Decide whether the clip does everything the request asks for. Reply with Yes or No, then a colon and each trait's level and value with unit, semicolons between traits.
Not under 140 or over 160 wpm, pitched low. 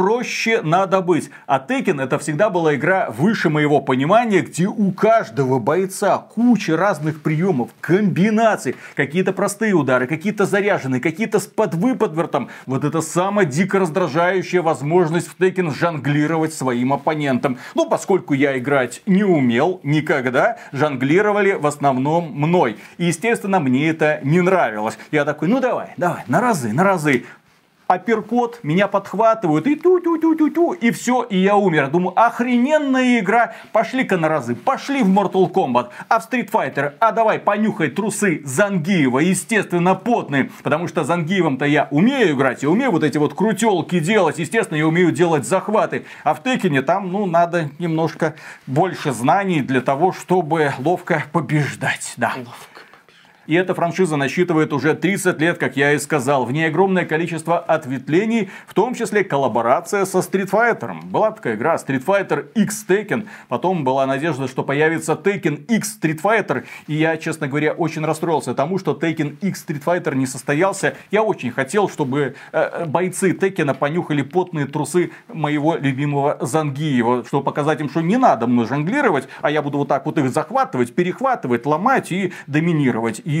No: average, 155 wpm; medium, 170 Hz